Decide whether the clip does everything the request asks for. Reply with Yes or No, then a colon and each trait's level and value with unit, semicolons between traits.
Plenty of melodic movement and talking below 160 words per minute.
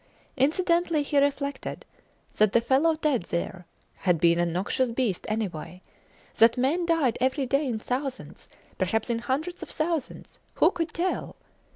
Yes: wide, 6.2 semitones; average, 150 wpm